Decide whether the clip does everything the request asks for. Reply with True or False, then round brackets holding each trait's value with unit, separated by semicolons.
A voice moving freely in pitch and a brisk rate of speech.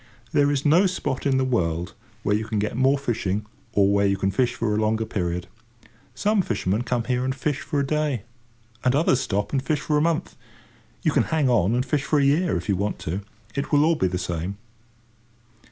True (6.0 semitones; 220 wpm)